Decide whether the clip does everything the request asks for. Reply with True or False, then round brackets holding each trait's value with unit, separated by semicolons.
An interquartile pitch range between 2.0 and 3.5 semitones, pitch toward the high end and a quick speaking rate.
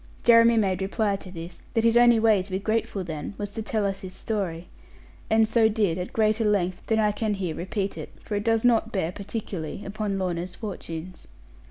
True (3.0 semitones; 205 Hz; 210 wpm)